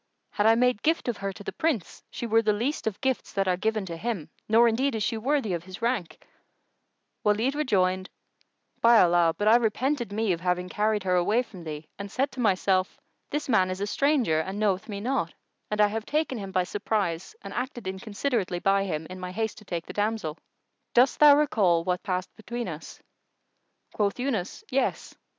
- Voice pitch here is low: No, high, 210 Hz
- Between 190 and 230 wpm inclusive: Yes, average, 200 wpm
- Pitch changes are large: No, average, 4.3 semitones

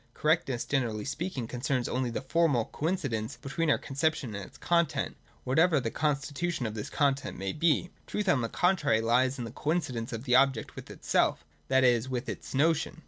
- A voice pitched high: No, low, 135 Hz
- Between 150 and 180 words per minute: No, average, 190 wpm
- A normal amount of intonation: Yes, average, 4.6 semitones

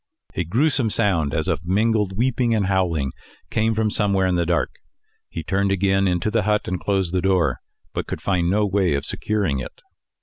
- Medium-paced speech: Yes, average, 195 wpm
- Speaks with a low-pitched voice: Yes, very low, 95 Hz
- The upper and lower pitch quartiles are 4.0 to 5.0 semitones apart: No, average, 3.6 semitones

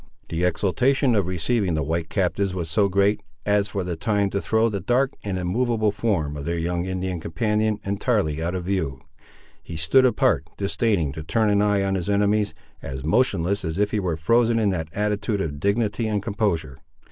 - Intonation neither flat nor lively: Yes, average, 3.9 semitones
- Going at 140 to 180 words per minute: No, average, 195 wpm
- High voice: No, low, 100 Hz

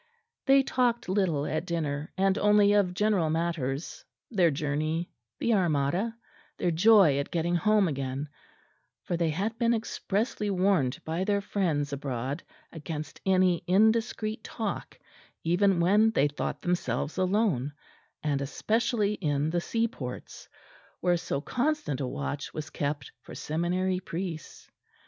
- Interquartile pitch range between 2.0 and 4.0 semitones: No, wide, 5.6 semitones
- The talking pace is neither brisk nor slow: No, slow, 130 wpm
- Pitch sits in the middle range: Yes, medium, 175 Hz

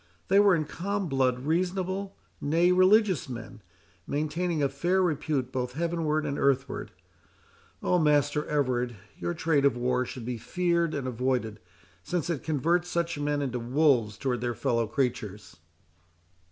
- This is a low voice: No, medium, 145 Hz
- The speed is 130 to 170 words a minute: Yes, average, 145 wpm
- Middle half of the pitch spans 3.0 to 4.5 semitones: No, average, 5.3 semitones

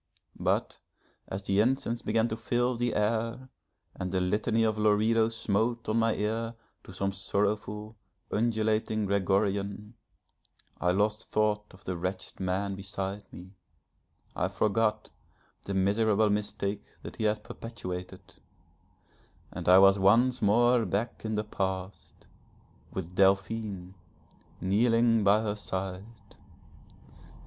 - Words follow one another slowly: Yes, slow, 120 wpm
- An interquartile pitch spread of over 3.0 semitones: No, narrow, 2.4 semitones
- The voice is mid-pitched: No, low, 105 Hz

